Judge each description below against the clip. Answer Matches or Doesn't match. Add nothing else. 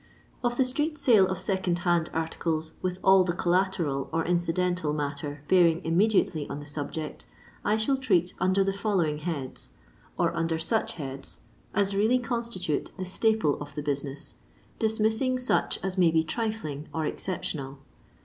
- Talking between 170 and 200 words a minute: Doesn't match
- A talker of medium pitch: Matches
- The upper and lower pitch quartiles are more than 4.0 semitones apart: Matches